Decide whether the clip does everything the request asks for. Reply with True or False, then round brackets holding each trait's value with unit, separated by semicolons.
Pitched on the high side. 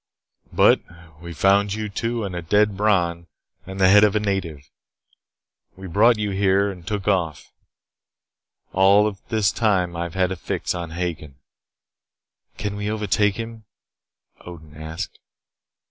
False (95 Hz)